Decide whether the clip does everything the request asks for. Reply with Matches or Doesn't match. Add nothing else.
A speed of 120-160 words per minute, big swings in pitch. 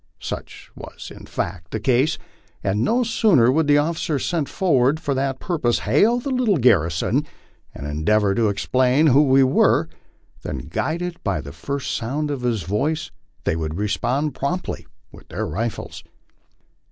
Matches